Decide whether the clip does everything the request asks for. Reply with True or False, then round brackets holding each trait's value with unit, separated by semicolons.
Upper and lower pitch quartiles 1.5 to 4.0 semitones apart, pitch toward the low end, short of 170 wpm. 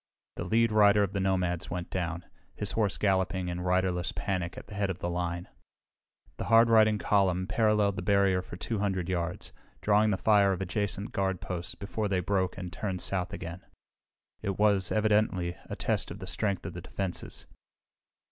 False (2.4 semitones; 95 Hz; 180 wpm)